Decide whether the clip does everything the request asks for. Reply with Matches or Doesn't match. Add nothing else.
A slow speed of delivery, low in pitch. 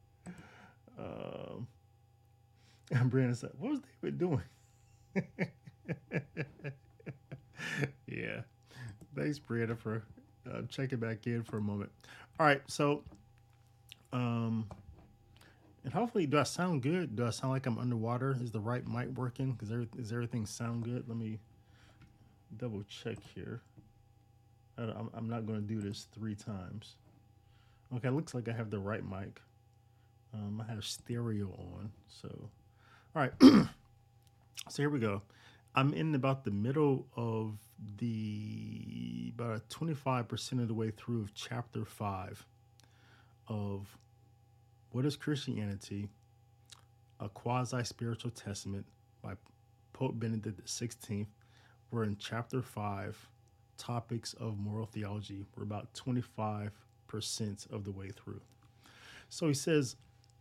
Matches